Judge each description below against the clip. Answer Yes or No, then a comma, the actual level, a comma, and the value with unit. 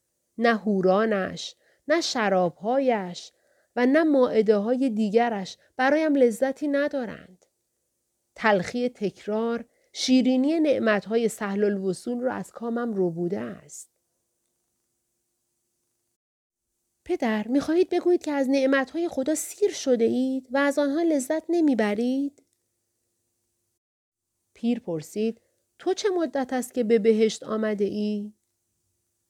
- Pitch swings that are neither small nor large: No, wide, 6.7 semitones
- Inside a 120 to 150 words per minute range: No, slow, 105 wpm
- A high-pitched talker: Yes, high, 230 Hz